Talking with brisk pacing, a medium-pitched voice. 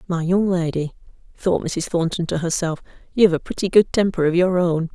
No: average, 195 wpm; medium, 175 Hz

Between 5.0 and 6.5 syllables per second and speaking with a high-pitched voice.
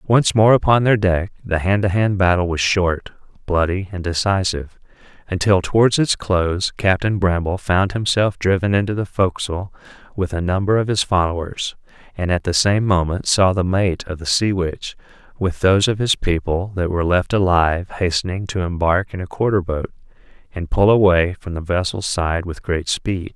No: 5.1 syllables/s; very low, 95 Hz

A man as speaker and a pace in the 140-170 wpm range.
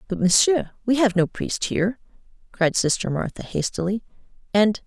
No: female; average, 150 wpm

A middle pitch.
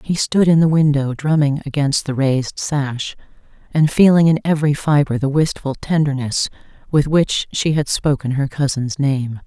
Yes: medium, 145 Hz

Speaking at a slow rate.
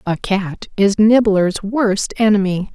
Yes: slow, 130 wpm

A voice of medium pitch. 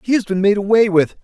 No: high, 205 Hz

